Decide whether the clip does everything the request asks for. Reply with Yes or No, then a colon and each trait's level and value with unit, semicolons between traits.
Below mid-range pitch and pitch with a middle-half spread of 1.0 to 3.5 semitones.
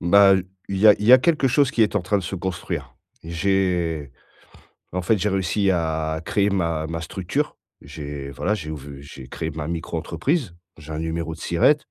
No: very low, 85 Hz; average, 4.1 semitones